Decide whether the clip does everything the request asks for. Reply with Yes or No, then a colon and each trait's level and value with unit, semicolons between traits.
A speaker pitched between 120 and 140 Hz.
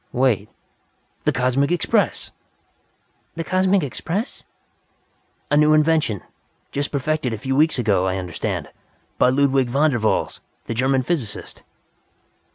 Yes: low, 135 Hz